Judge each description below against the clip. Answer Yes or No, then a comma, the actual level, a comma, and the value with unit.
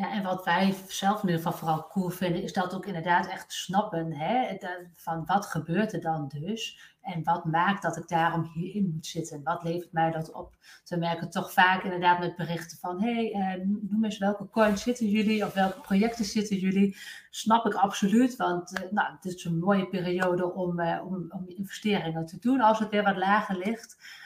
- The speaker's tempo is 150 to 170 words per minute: No, fast, 200 wpm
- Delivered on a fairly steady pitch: No, average, 3.0 semitones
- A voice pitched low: No, medium, 185 Hz